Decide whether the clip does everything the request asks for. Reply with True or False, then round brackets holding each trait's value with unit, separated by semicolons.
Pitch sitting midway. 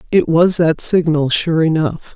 True (160 Hz)